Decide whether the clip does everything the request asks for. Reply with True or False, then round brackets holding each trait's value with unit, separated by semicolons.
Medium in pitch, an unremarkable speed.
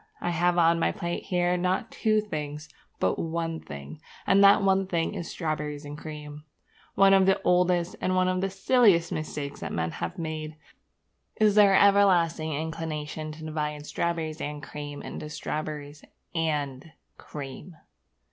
True (165 Hz; 145 wpm)